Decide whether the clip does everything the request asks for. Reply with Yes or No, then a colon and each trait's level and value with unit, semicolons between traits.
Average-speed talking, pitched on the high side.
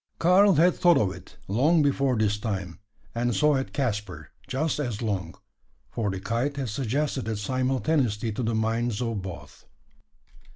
No: average, 160 wpm; low, 120 Hz